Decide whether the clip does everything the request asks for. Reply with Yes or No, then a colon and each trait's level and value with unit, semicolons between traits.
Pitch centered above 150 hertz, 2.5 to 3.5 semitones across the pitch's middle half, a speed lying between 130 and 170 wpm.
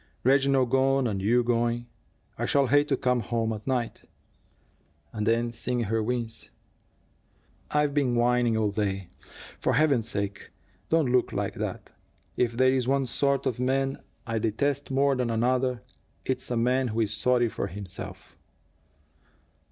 No: low, 125 Hz; average, 2.8 semitones; average, 150 wpm